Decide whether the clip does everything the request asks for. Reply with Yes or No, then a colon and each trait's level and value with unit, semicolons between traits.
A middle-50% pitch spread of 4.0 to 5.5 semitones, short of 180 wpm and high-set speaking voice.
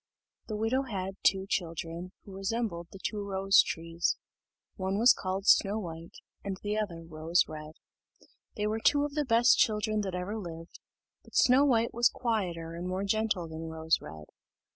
Yes: average, 4.5 semitones; average, 170 wpm; high, 195 Hz